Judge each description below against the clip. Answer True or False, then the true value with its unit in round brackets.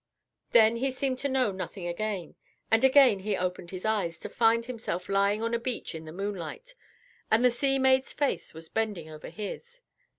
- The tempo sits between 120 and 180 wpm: False (190 wpm)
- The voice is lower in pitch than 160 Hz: False (220 Hz)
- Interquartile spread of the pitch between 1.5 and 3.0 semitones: False (5.5 semitones)